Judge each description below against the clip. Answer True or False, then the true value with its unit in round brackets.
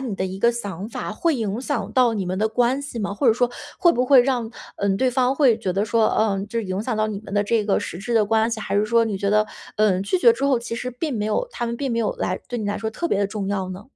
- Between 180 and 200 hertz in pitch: False (220 Hz)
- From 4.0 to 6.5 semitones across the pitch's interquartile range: False (3.4 semitones)